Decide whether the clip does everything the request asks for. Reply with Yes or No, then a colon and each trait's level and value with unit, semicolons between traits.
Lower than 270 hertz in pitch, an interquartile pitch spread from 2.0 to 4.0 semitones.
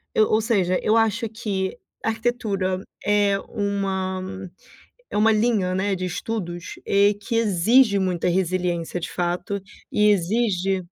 Yes: high, 200 Hz; average, 2.9 semitones